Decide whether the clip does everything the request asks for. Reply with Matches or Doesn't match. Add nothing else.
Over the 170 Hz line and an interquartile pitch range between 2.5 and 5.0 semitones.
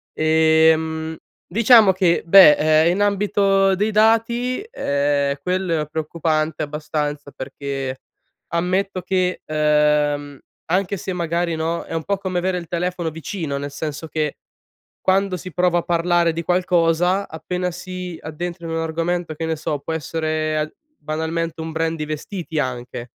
Doesn't match